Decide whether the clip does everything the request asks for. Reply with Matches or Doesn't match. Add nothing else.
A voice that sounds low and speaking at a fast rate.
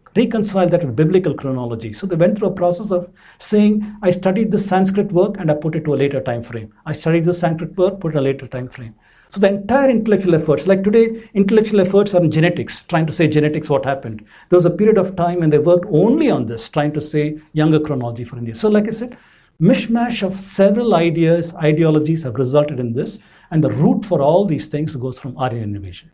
Doesn't match